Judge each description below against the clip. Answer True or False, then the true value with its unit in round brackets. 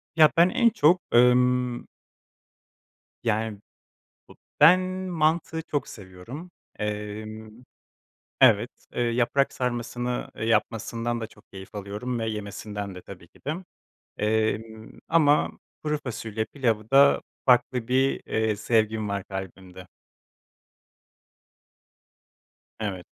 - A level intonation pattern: False (3.4 semitones)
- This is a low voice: True (115 Hz)